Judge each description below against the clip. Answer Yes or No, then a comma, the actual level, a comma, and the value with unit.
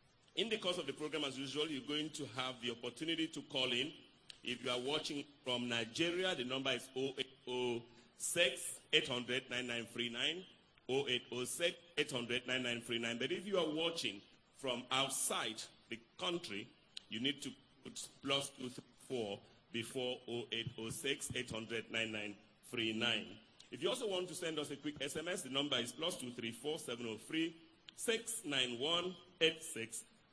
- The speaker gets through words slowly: Yes, slow, 120 wpm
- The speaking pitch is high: No, low, 130 Hz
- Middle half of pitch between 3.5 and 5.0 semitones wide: Yes, average, 4.5 semitones